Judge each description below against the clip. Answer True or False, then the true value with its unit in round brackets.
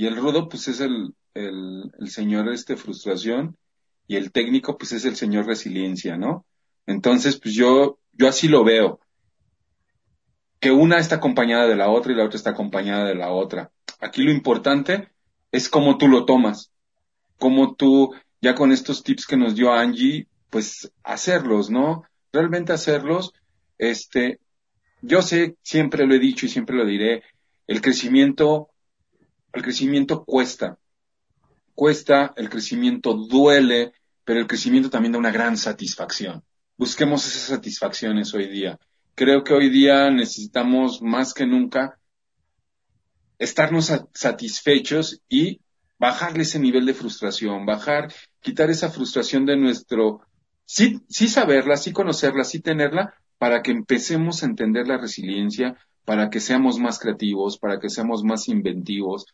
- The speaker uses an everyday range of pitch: False (5.7 semitones)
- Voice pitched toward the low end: True (130 Hz)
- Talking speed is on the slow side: False (145 wpm)